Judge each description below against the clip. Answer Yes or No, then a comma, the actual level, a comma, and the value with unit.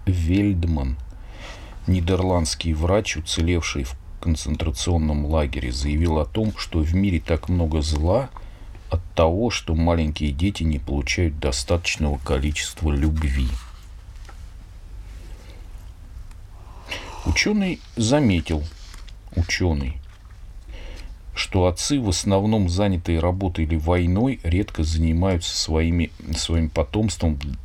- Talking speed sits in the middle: No, slow, 90 wpm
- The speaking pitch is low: Yes, very low, 85 Hz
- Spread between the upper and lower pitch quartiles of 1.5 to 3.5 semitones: Yes, average, 2.7 semitones